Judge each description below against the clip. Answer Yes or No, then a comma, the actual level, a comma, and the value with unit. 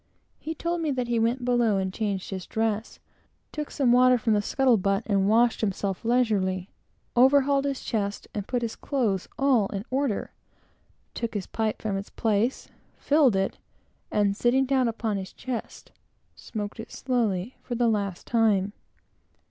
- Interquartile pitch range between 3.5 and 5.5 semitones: Yes, average, 3.9 semitones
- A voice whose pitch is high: Yes, high, 225 Hz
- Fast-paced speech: No, average, 165 wpm